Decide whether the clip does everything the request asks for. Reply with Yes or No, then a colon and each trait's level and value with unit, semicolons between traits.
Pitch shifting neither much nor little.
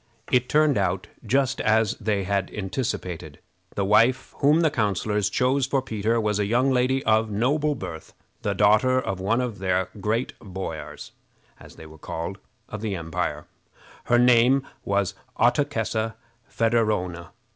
Yes: average, 4.5 semitones